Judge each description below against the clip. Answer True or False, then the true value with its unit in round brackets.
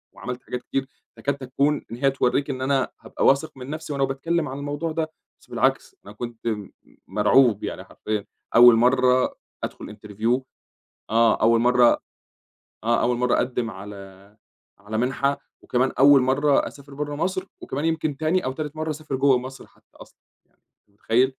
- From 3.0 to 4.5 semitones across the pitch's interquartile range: True (3.4 semitones)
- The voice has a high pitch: False (130 Hz)